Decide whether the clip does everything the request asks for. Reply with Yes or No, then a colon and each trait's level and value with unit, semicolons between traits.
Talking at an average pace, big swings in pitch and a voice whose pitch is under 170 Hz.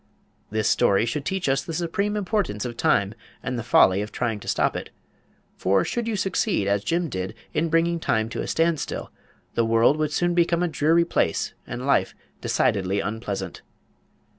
Yes: average, 180 wpm; wide, 8.5 semitones; medium, 140 Hz